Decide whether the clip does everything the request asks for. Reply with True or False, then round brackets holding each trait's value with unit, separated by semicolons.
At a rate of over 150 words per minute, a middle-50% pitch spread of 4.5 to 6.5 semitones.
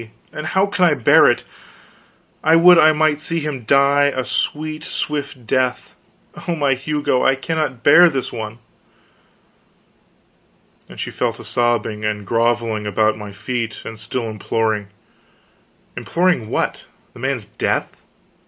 False (140 wpm; 5.5 semitones)